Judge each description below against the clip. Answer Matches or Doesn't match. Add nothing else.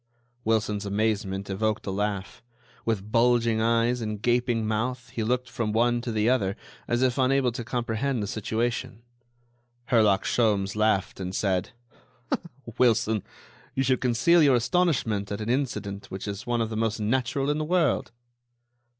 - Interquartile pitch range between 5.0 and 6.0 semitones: Doesn't match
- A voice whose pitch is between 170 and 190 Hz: Doesn't match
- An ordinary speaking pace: Matches